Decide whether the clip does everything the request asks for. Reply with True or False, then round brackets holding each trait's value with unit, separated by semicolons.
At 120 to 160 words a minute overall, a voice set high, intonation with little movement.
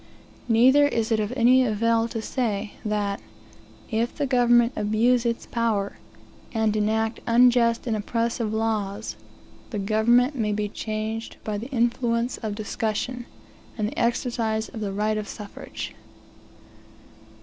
True (135 wpm; 225 Hz; 1.9 semitones)